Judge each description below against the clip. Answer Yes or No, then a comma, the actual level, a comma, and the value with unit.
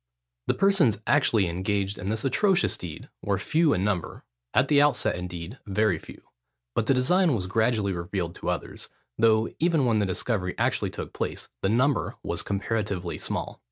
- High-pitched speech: No, low, 110 Hz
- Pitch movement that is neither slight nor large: No, wide, 6.0 semitones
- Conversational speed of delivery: Yes, average, 170 wpm